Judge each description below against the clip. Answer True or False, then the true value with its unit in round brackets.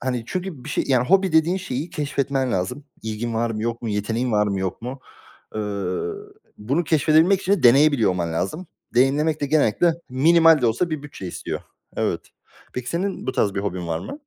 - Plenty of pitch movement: True (6.3 semitones)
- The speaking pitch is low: True (130 Hz)